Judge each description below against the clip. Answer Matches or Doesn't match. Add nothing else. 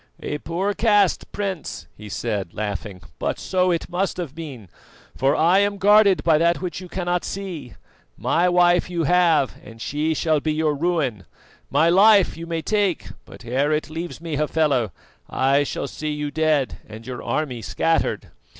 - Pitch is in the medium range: Matches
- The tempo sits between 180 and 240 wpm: Doesn't match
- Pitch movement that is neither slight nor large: Matches